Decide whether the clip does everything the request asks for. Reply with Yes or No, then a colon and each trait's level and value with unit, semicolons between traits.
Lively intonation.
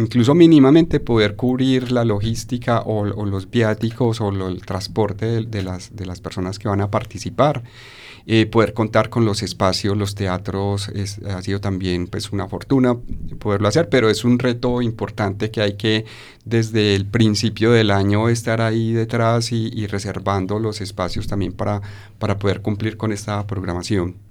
No: narrow, 2.5 semitones